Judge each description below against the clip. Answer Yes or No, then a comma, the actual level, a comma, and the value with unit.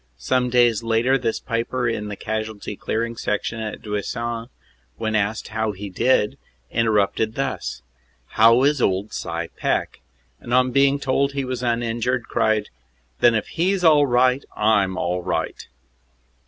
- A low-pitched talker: Yes, low, 115 Hz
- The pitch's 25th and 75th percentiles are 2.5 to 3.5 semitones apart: Yes, average, 3.0 semitones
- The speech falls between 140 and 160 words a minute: Yes, average, 155 wpm